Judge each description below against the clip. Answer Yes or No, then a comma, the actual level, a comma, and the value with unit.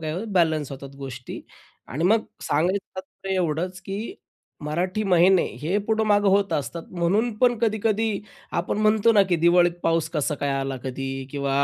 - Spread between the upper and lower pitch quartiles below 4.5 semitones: No, average, 5.1 semitones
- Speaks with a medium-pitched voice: Yes, medium, 180 Hz